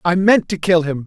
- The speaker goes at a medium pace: No, fast, 280 wpm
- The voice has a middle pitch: Yes, medium, 175 Hz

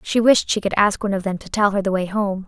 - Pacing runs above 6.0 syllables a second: Yes, 6.3 syllables/s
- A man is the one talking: No, female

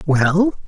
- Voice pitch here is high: No, medium, 175 Hz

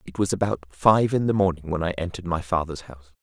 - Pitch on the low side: Yes, very low, 90 Hz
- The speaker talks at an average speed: No, fast, 240 wpm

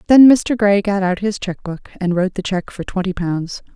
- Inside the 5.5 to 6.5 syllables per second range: No, 5.0 syllables/s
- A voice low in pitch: No, high, 200 Hz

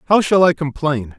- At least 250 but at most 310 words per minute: No, average, 200 wpm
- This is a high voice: No, medium, 155 Hz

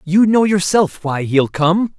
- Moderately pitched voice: Yes, medium, 180 Hz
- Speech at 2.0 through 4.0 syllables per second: Yes, 3.7 syllables/s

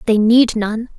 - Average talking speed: Yes, average, 185 wpm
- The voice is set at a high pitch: Yes, high, 225 Hz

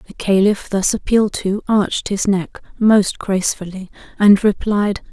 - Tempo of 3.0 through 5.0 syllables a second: Yes, 4.5 syllables/s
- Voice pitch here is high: Yes, high, 200 Hz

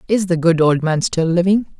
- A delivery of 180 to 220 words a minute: No, fast, 235 wpm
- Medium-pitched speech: Yes, medium, 175 Hz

